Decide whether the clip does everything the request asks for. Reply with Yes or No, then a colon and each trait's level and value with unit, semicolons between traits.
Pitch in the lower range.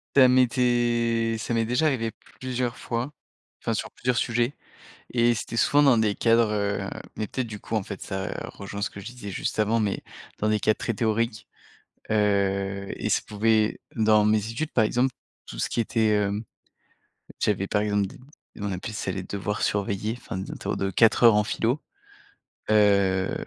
Yes: low, 110 Hz